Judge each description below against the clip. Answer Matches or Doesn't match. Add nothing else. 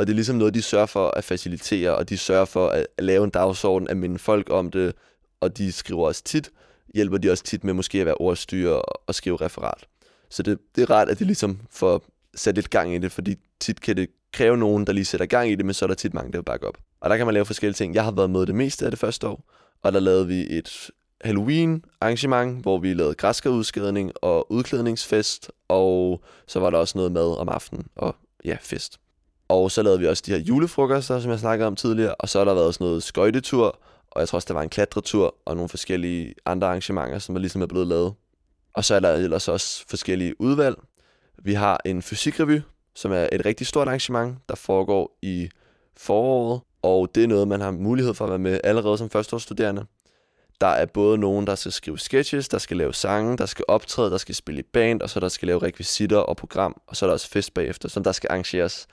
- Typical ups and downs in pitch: Matches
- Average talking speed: Doesn't match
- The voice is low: Matches